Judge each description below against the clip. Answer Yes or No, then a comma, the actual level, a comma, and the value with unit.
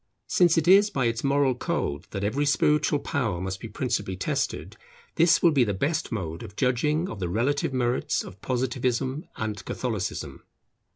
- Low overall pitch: Yes, low, 125 Hz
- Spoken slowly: No, average, 170 wpm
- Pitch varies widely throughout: Yes, wide, 6.0 semitones